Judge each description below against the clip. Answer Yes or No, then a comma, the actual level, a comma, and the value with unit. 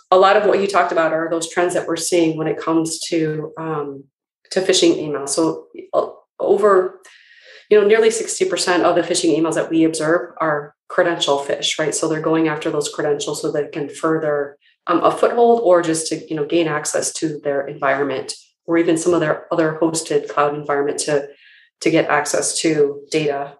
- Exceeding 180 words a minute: Yes, average, 200 wpm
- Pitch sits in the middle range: Yes, medium, 160 Hz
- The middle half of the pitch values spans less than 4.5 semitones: Yes, average, 2.9 semitones